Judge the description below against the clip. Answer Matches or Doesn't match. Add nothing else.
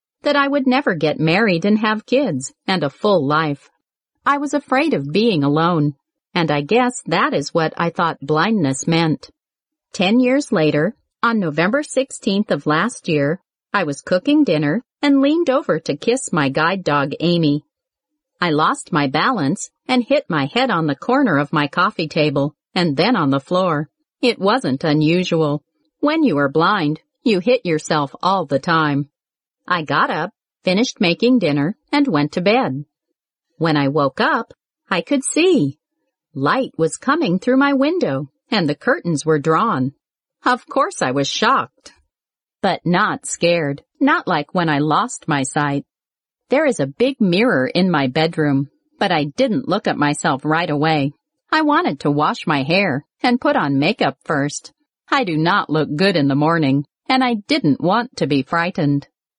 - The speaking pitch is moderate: Matches